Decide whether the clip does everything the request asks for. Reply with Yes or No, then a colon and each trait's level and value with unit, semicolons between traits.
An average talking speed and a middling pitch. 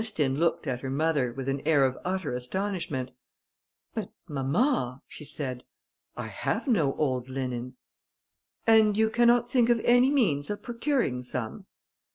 Yes: average, 150 wpm; medium, 150 Hz